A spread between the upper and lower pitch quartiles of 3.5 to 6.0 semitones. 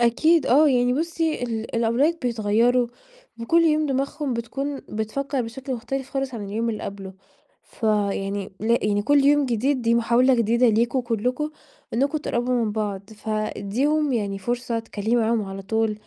Yes: average, 3.8 semitones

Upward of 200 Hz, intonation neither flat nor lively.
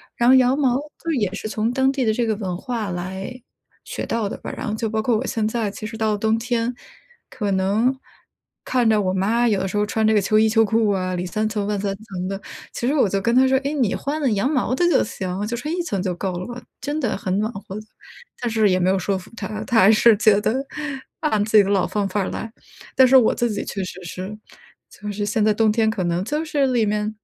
Yes: high, 215 Hz; average, 3.4 semitones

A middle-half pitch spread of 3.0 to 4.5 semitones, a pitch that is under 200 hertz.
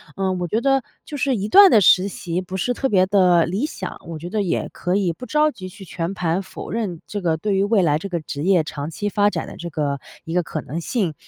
Yes: average, 3.6 semitones; medium, 185 Hz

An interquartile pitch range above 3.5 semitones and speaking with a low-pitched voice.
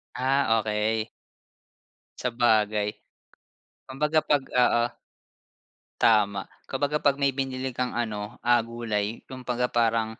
No: average, 3.2 semitones; low, 120 Hz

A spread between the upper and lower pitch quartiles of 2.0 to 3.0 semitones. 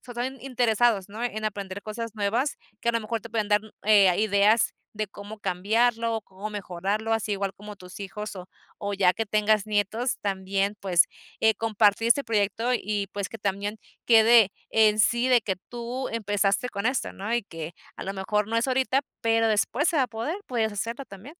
Yes: narrow, 2.4 semitones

